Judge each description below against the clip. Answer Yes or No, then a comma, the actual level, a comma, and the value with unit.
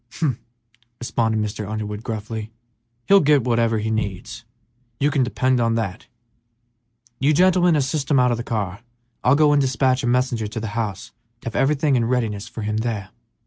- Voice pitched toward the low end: Yes, low, 115 Hz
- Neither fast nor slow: Yes, average, 180 wpm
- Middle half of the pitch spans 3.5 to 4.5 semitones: Yes, average, 3.8 semitones